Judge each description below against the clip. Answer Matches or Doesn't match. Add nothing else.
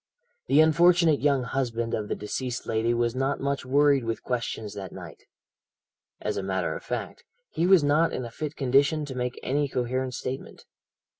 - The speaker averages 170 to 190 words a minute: Matches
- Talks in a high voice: Doesn't match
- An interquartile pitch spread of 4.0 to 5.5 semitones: Doesn't match